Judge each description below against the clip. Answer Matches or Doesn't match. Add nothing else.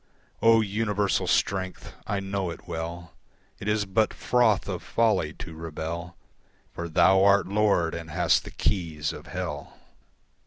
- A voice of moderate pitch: Doesn't match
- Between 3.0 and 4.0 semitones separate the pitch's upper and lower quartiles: Matches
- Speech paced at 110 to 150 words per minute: Matches